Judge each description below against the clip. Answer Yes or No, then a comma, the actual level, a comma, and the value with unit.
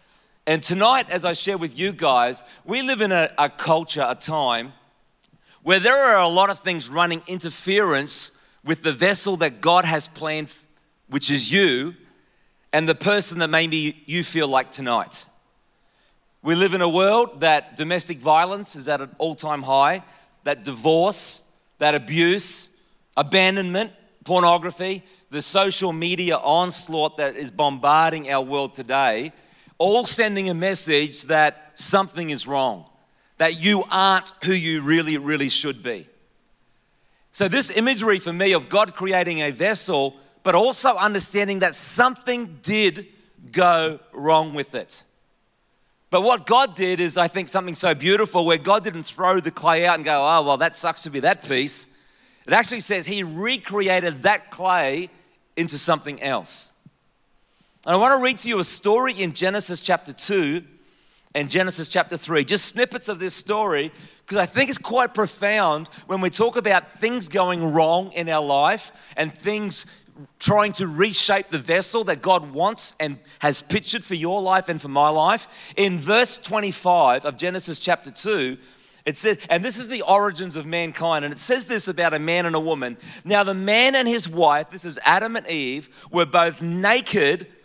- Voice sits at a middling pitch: Yes, medium, 175 Hz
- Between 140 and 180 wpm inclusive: Yes, average, 170 wpm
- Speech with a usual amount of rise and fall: Yes, average, 4.3 semitones